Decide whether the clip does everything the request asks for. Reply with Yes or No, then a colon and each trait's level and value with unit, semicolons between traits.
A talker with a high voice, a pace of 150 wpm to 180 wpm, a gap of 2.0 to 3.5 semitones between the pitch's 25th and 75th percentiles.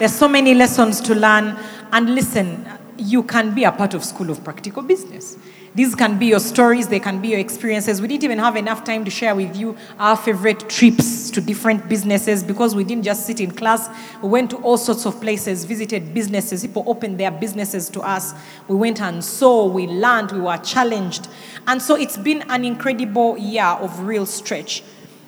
No: high, 215 Hz; average, 200 wpm; average, 2.8 semitones